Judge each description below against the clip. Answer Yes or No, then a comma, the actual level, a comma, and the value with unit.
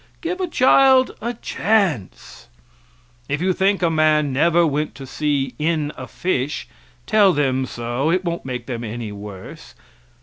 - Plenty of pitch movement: Yes, wide, 6.3 semitones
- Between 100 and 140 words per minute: No, average, 155 wpm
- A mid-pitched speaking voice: Yes, medium, 150 Hz